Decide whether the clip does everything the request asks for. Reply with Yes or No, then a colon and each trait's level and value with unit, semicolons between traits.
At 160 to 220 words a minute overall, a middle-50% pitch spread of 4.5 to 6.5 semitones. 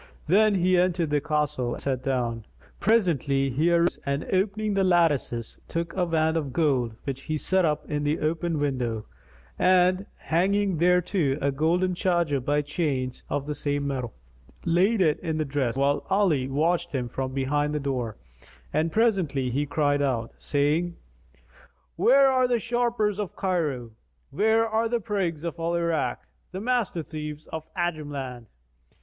Yes: average, 165 wpm; average, 4.8 semitones